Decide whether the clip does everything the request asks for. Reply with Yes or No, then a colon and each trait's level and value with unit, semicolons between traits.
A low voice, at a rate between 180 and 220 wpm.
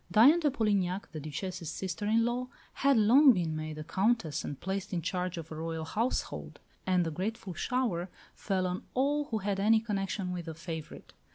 No: high, 190 Hz; average, 190 wpm